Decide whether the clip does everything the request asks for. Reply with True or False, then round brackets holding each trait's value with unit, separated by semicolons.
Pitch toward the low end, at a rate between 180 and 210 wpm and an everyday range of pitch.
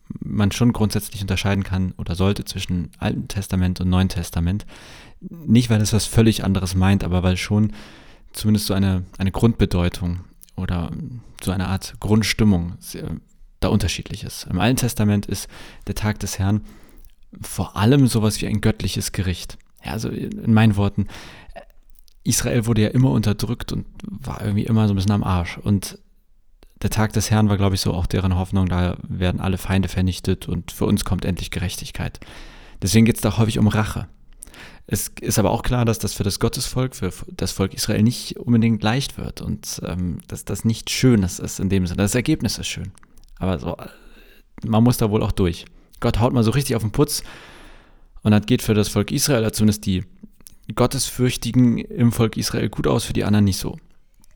True (105 Hz; 185 wpm; 3.4 semitones)